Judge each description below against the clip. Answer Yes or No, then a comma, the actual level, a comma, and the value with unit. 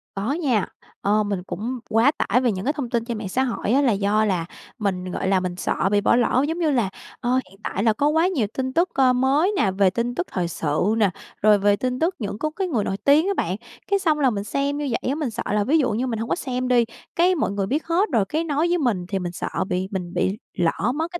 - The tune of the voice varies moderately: No, wide, 6.4 semitones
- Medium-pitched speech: No, high, 240 Hz